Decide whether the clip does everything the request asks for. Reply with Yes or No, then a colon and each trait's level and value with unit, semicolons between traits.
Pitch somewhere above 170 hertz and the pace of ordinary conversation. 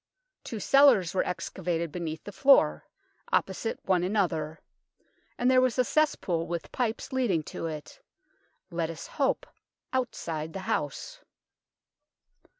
No: medium, 185 Hz; slow, 125 wpm